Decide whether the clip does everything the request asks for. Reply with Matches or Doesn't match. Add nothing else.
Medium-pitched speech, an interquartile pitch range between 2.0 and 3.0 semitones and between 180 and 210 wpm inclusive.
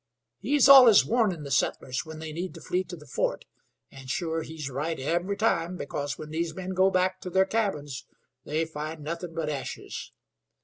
Doesn't match